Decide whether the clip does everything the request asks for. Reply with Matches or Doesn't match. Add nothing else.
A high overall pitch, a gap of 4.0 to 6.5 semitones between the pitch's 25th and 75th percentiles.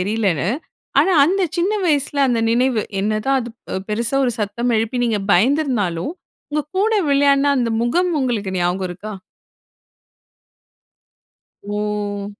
Matches